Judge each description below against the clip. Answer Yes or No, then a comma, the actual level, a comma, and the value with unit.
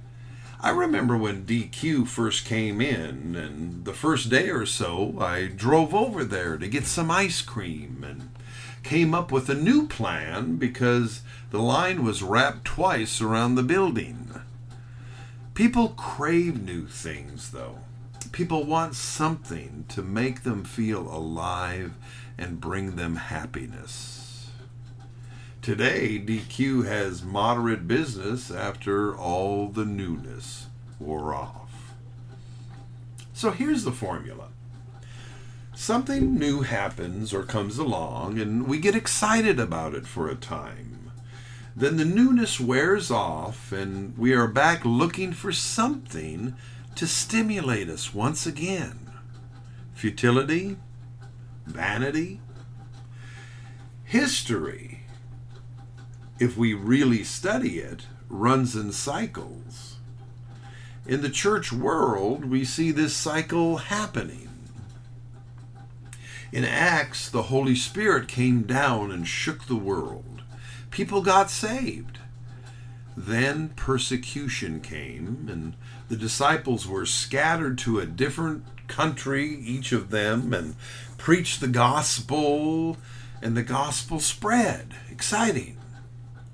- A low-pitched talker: Yes, low, 120 Hz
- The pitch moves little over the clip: Yes, narrow, 1.9 semitones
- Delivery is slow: Yes, slow, 110 wpm